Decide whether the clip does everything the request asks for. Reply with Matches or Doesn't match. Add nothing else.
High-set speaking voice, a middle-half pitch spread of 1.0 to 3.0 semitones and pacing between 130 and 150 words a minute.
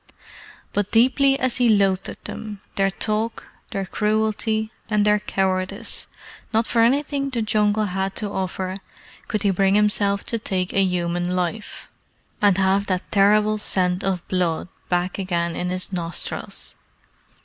Matches